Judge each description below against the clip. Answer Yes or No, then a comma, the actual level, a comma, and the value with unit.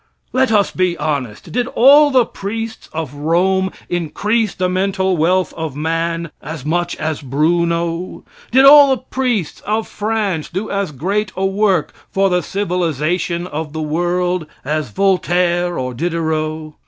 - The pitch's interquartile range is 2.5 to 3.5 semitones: No, average, 3.9 semitones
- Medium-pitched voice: Yes, medium, 175 Hz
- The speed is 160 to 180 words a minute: No, average, 145 wpm